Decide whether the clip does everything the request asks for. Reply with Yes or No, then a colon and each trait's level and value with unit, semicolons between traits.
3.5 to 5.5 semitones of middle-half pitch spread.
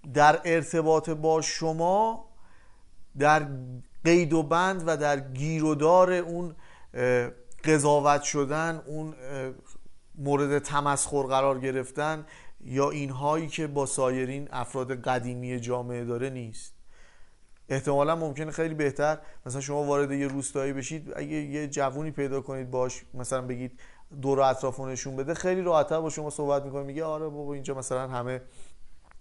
No: average, 3.1 semitones